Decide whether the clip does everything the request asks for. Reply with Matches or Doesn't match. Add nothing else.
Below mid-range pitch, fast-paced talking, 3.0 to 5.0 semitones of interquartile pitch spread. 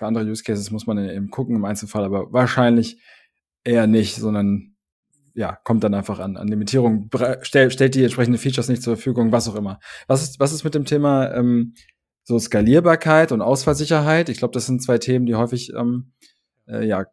Matches